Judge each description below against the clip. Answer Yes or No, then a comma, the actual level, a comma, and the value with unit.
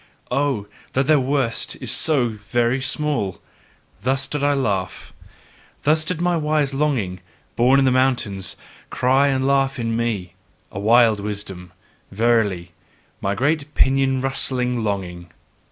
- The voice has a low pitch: Yes, low, 125 Hz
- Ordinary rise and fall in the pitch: Yes, average, 4.9 semitones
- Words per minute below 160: Yes, slow, 135 wpm